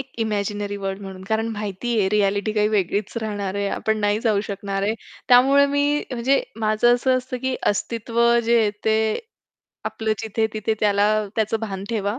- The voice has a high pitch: Yes, high, 215 Hz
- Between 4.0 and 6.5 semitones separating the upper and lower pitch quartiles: No, narrow, 2.5 semitones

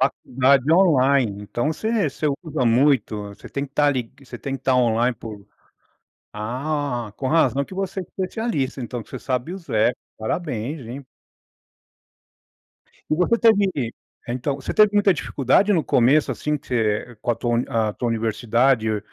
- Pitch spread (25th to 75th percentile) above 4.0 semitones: Yes, average, 4.5 semitones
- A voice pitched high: No, low, 130 Hz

